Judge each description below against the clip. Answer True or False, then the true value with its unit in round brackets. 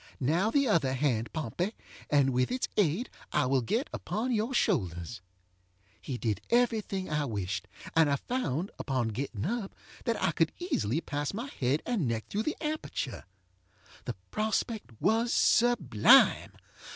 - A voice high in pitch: False (150 Hz)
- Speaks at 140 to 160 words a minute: True (150 wpm)